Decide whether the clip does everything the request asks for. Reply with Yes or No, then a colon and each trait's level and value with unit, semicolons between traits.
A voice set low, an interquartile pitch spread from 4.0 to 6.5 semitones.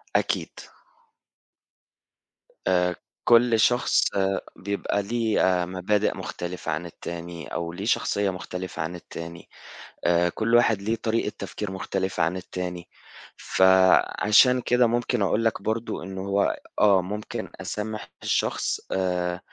No: very low, 95 Hz; average, 3.6 semitones